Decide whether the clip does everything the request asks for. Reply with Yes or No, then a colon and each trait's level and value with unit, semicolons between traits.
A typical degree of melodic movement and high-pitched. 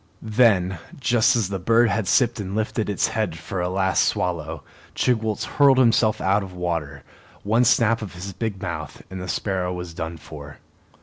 No: average, 4.0 semitones; very low, 95 Hz